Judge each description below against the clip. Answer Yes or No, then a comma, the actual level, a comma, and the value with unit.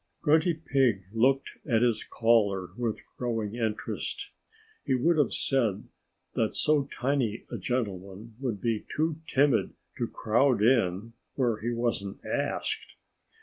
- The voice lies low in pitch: Yes, low, 120 Hz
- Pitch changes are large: No, average, 4.0 semitones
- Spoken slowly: Yes, slow, 130 wpm